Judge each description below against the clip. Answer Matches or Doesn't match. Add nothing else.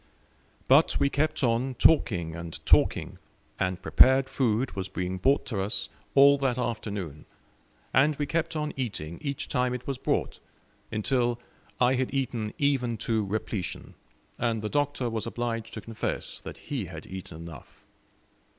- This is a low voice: Matches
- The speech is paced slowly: Doesn't match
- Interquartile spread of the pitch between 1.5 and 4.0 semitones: Doesn't match